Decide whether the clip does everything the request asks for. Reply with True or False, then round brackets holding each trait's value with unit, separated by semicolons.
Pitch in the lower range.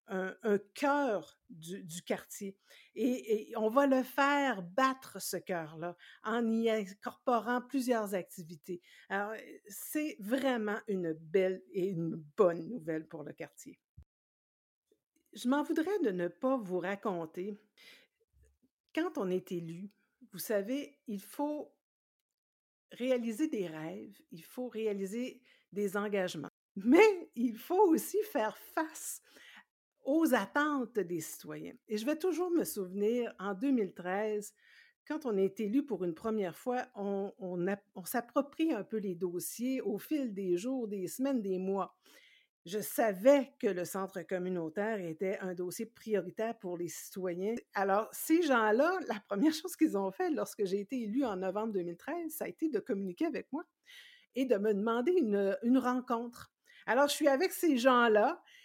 False (215 Hz)